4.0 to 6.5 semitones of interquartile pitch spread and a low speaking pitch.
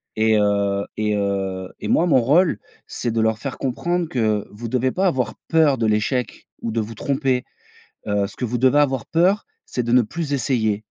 Yes: average, 4.3 semitones; low, 120 Hz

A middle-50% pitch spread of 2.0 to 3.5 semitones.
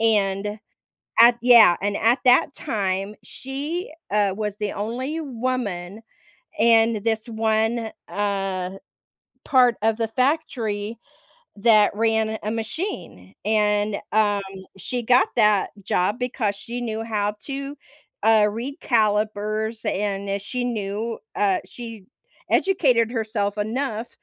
Yes: average, 2.7 semitones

